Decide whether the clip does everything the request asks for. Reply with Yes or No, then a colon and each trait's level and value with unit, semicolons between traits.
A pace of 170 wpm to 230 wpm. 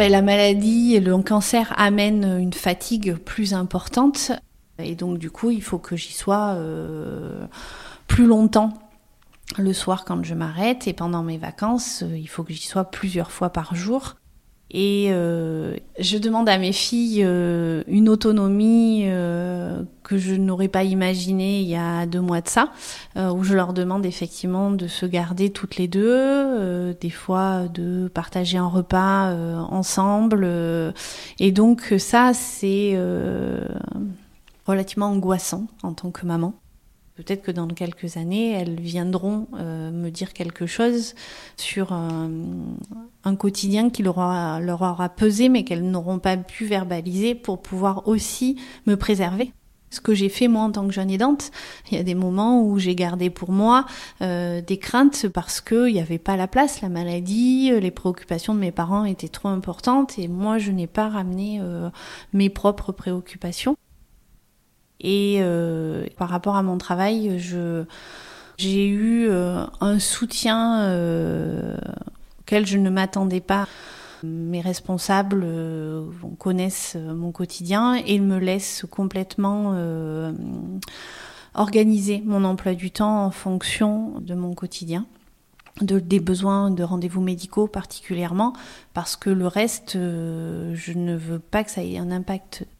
No: average, 155 wpm